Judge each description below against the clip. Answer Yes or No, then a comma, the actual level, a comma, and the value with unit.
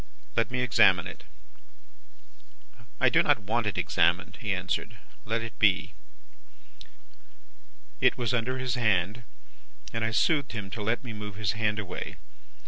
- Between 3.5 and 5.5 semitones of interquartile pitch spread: No, average, 3.0 semitones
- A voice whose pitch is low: Yes, low, 110 Hz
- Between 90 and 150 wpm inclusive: Yes, average, 145 wpm